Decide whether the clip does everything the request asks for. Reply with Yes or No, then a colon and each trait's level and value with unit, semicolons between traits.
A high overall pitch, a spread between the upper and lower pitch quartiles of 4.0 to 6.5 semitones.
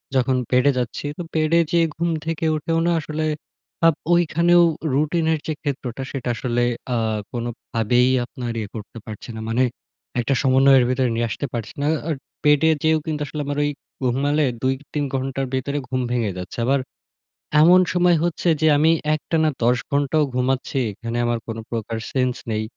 No: low, 135 Hz; average, 4.3 semitones